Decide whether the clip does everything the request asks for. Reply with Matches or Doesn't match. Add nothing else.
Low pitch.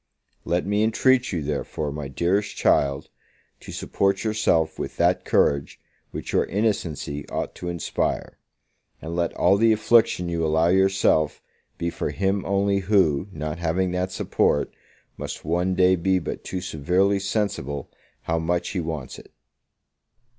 Matches